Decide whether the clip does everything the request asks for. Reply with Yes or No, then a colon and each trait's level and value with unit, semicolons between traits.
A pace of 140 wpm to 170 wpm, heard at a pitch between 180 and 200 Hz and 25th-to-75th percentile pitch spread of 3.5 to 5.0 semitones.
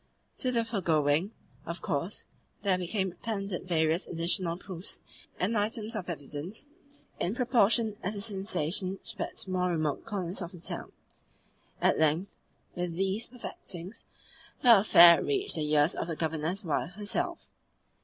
Yes: average, 145 wpm; medium, 185 Hz; average, 4.0 semitones